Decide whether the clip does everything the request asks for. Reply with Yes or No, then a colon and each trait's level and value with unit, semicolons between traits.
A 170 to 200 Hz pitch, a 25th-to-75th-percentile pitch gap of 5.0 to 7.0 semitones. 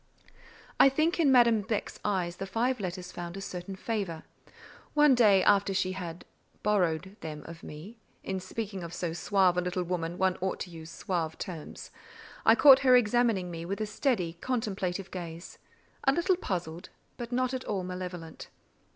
No: high, 190 Hz; average, 4.5 semitones